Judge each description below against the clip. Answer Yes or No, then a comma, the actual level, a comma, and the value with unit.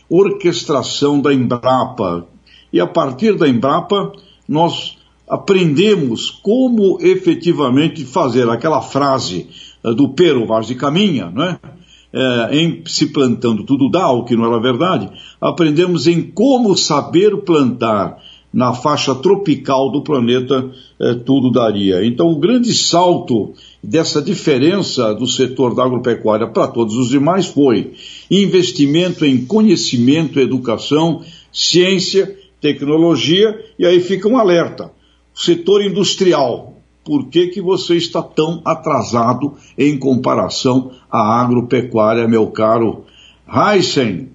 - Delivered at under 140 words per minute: Yes, slow, 120 wpm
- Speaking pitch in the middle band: Yes, medium, 150 Hz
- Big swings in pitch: Yes, wide, 5.8 semitones